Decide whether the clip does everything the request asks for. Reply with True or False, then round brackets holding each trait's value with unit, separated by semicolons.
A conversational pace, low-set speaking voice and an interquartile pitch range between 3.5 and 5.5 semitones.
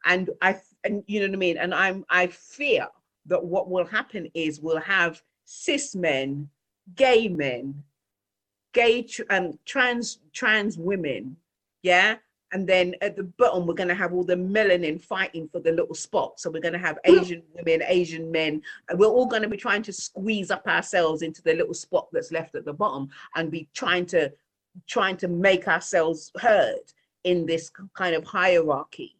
False (185 wpm; 180 Hz; 4.0 semitones)